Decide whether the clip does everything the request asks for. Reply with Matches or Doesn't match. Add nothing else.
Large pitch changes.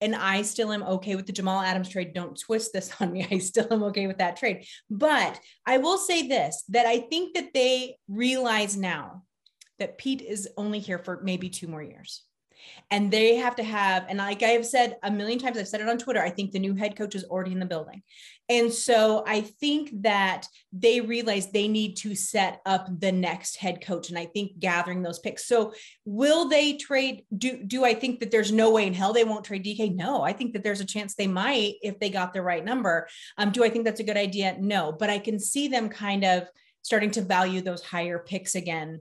Doesn't match